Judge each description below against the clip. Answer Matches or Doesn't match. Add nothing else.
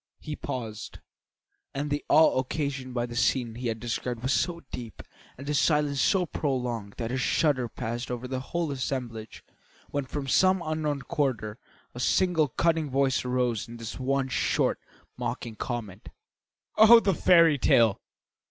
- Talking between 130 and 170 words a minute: Matches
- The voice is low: Matches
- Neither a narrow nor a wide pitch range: Matches